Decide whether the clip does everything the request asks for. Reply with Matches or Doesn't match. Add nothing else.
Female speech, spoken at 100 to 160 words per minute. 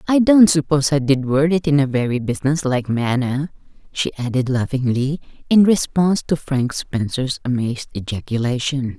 Matches